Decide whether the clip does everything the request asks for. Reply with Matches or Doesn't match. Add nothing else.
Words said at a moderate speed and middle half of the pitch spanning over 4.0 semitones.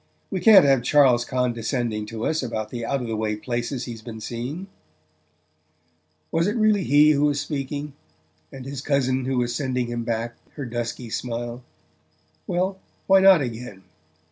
Doesn't match